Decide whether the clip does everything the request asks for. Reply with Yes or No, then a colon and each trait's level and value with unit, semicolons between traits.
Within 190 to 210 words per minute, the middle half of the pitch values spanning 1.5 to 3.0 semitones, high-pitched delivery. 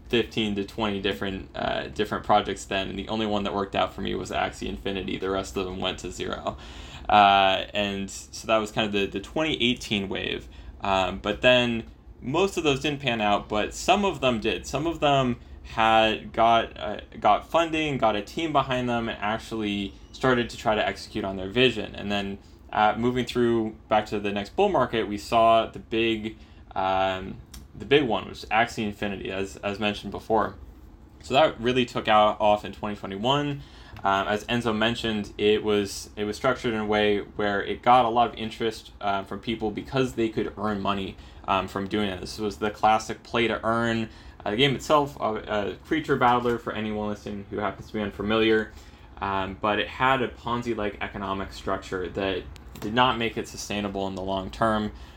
No: average, 200 wpm; average, 2.7 semitones; low, 105 Hz